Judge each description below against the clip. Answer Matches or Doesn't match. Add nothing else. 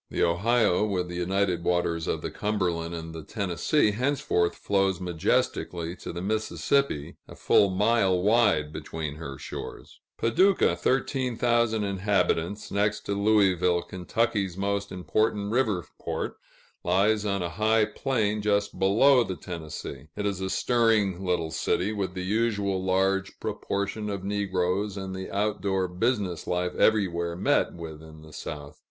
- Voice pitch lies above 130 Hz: Doesn't match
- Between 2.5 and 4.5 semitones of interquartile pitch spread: Matches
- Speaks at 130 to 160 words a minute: Matches